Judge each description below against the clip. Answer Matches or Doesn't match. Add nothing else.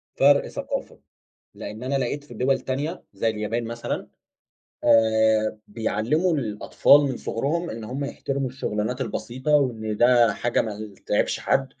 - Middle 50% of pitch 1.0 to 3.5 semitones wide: Doesn't match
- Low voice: Matches